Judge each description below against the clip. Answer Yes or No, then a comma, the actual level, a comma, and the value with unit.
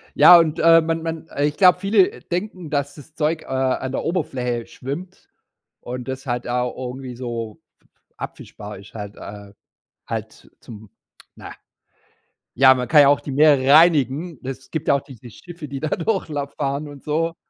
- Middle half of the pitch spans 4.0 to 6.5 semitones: Yes, average, 4.4 semitones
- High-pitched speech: No, medium, 140 Hz